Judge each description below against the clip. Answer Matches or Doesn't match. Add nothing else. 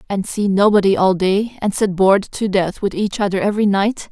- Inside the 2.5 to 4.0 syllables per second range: Doesn't match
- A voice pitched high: Matches